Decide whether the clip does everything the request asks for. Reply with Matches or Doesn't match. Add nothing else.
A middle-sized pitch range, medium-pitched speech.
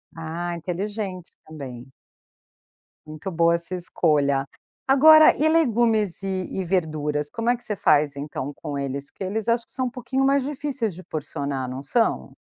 Doesn't match